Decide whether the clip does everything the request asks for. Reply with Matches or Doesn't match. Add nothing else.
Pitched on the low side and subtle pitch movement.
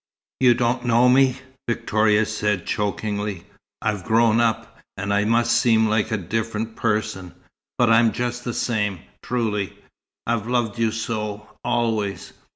Matches